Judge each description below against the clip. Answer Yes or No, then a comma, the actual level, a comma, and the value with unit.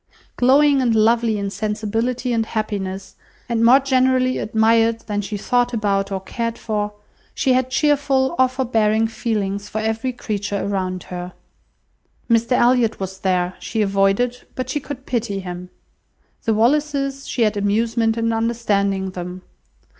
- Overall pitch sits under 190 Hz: No, high, 225 Hz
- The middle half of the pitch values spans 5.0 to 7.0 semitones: No, average, 3.7 semitones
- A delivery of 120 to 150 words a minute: Yes, average, 145 wpm